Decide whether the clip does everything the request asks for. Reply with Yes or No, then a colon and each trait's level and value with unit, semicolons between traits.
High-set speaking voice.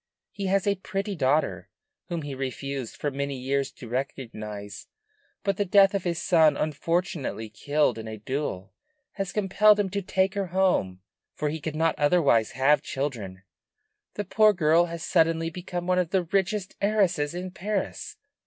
No: medium, 165 Hz